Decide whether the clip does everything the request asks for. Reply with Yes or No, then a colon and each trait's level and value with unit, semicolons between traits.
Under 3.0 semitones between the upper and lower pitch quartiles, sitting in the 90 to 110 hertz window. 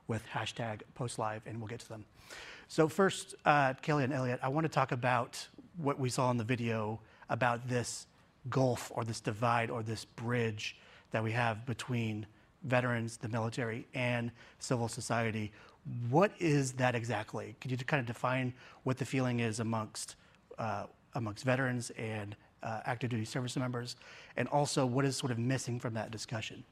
No: narrow, 2.6 semitones; low, 120 Hz